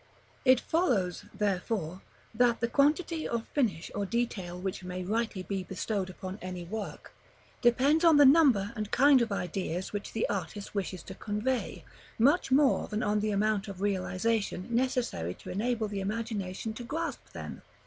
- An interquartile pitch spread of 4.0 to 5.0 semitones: Yes, average, 4.3 semitones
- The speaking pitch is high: Yes, high, 215 Hz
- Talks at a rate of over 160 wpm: Yes, average, 170 wpm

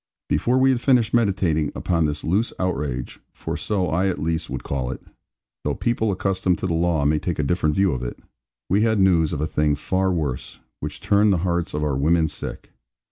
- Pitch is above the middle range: No, very low, 85 Hz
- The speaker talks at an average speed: No, fast, 210 wpm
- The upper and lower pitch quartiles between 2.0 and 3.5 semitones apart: No, average, 4.3 semitones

